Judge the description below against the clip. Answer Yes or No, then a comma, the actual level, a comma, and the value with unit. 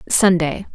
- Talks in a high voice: No, medium, 175 Hz